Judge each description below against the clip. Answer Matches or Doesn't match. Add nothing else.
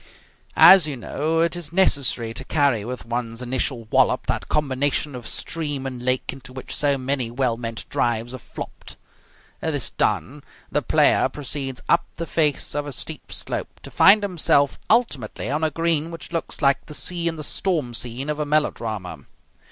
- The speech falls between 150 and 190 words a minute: Matches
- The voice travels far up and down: Doesn't match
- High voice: Doesn't match